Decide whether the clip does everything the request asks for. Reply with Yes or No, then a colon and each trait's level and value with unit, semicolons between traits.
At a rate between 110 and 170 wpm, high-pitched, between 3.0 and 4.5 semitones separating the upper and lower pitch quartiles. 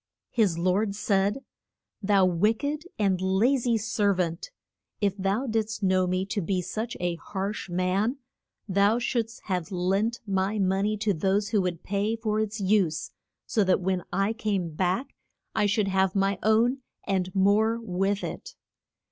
No: average, 165 wpm; high, 200 Hz; narrow, 2.6 semitones